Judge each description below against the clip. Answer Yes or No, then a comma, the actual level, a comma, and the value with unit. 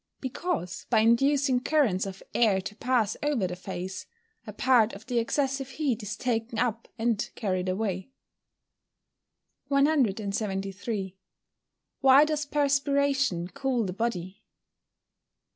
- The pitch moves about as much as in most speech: No, wide, 5.8 semitones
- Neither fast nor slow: No, slow, 120 wpm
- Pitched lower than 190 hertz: No, high, 230 Hz